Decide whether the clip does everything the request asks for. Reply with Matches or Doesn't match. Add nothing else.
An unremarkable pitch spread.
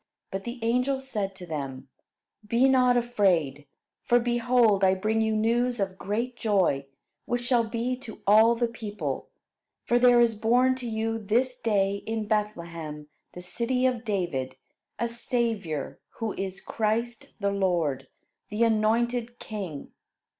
Matches